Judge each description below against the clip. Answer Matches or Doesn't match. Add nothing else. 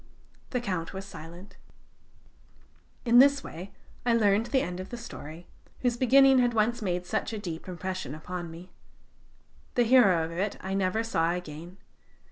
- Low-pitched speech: Doesn't match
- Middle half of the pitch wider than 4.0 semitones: Matches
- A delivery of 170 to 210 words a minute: Doesn't match